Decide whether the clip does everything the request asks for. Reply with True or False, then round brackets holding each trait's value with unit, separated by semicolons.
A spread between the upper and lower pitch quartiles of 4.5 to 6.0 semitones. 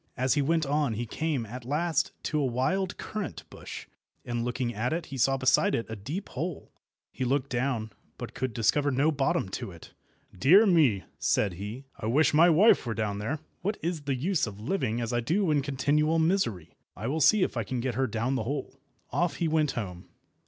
True (5.2 semitones)